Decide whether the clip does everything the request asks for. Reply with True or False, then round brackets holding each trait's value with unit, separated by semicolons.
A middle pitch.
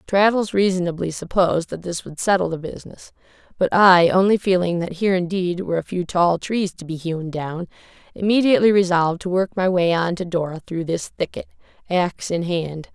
True (180 Hz)